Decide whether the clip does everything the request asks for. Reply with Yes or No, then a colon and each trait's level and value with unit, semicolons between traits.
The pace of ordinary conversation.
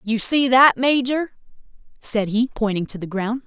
Yes: average, 175 wpm